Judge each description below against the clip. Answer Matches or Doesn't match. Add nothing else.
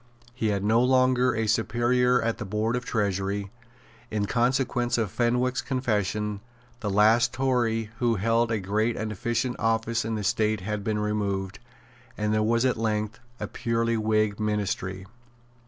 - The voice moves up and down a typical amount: Doesn't match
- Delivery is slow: Doesn't match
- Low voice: Matches